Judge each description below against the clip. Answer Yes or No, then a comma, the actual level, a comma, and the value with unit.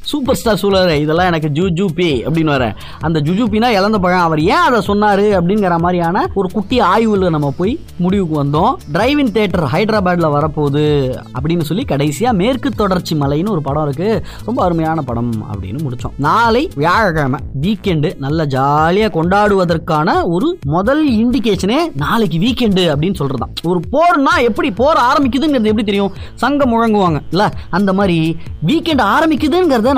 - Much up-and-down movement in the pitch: Yes, wide, 6.0 semitones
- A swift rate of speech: Yes, fast, 145 wpm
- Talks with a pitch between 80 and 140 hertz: No, medium, 185 Hz